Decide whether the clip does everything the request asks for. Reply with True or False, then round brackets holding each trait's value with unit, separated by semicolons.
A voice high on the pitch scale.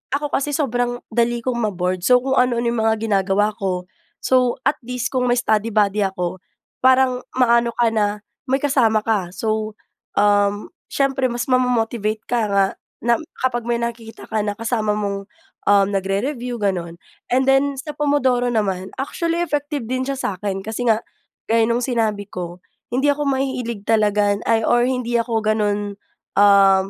True (230 Hz)